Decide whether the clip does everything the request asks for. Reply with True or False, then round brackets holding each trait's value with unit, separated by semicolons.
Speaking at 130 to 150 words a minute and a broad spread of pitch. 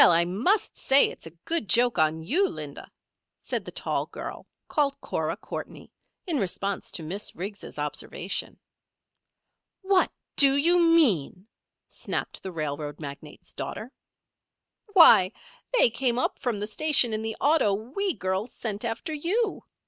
True (140 wpm; 8.7 semitones)